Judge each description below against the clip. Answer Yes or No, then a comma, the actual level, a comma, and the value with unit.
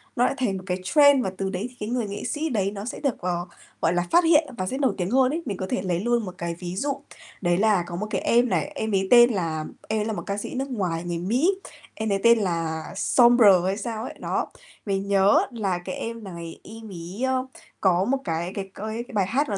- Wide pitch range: No, average, 4.7 semitones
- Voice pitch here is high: Yes, high, 205 Hz